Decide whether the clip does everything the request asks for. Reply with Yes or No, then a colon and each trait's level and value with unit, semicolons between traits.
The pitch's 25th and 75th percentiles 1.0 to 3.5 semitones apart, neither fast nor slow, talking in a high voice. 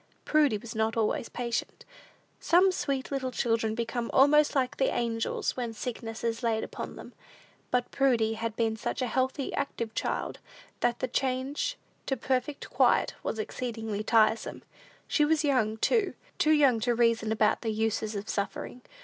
Yes: average, 3.2 semitones; average, 160 wpm; high, 235 Hz